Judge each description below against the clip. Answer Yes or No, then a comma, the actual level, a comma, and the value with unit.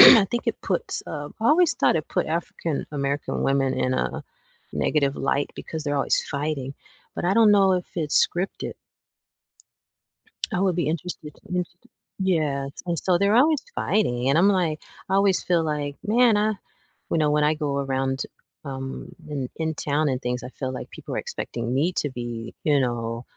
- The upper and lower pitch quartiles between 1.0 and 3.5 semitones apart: No, average, 4.9 semitones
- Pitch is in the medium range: Yes, medium, 150 Hz